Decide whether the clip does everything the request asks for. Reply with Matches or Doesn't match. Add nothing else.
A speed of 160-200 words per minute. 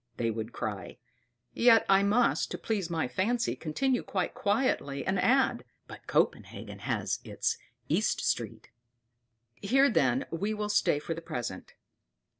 Doesn't match